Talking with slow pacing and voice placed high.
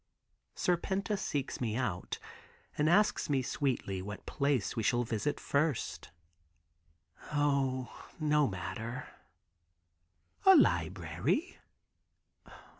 No: slow, 90 wpm; medium, 140 Hz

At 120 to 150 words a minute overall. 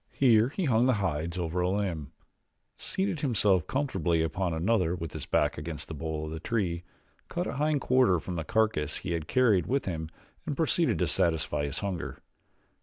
No: average, 185 wpm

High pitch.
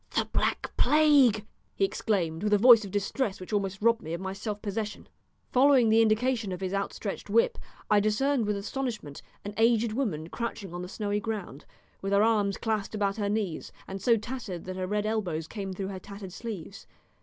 Yes: high, 210 Hz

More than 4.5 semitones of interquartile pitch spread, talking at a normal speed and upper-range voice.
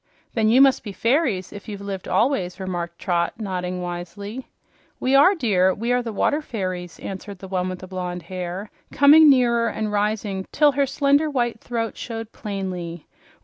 Yes: average, 4.9 semitones; average, 175 wpm; high, 205 Hz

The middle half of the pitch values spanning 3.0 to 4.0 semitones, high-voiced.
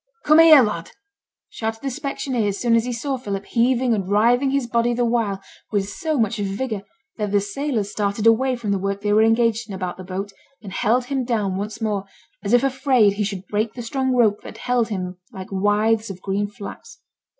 Yes: average, 3.5 semitones; high, 220 Hz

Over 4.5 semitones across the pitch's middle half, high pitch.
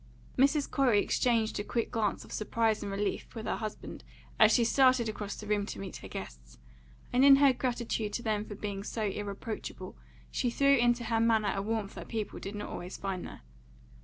No: average, 2.7 semitones; high, 220 Hz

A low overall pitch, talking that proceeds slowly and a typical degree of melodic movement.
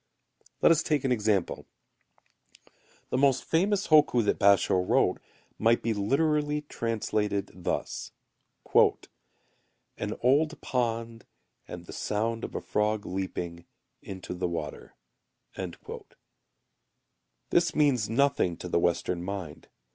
No: low, 115 Hz; slow, 110 wpm; wide, 6.7 semitones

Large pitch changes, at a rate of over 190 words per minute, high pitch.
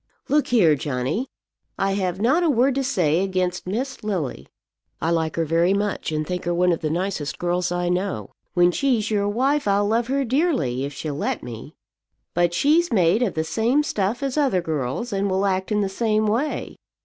Yes: wide, 5.8 semitones; average, 200 wpm; high, 195 Hz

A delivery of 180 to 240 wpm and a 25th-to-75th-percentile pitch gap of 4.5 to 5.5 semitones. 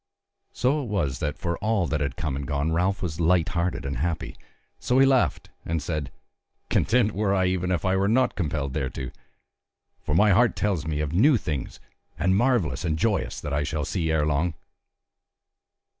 Yes: average, 190 wpm; average, 5.0 semitones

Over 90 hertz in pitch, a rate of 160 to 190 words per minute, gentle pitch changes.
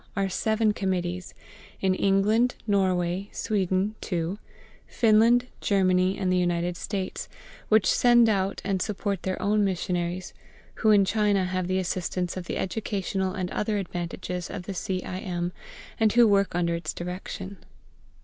No: high, 190 Hz; average, 150 wpm; narrow, 2.2 semitones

